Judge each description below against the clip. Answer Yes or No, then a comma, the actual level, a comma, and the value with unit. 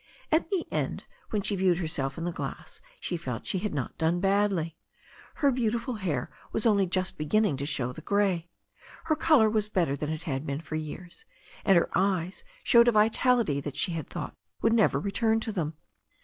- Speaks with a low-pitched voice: No, medium, 185 Hz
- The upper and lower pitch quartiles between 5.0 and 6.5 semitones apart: Yes, wide, 5.5 semitones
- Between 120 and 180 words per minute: No, average, 200 wpm